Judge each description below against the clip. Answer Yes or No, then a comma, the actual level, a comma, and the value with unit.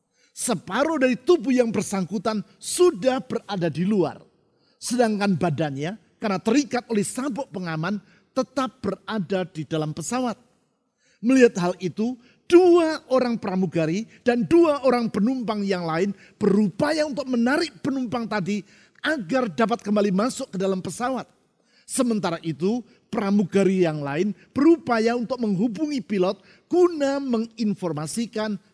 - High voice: Yes, high, 220 Hz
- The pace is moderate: Yes, average, 115 wpm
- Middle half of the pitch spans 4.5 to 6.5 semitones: Yes, average, 4.8 semitones